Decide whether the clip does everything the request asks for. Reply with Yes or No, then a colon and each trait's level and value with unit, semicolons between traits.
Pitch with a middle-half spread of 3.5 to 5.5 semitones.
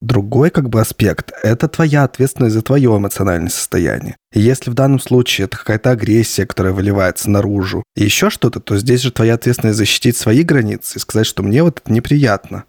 Yes: average, 4.3 semitones